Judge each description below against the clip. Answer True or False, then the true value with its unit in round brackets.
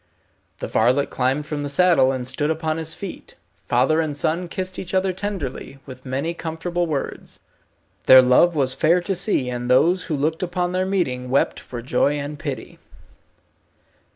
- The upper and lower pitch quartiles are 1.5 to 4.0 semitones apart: False (5.1 semitones)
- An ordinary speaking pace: True (170 wpm)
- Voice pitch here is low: False (155 Hz)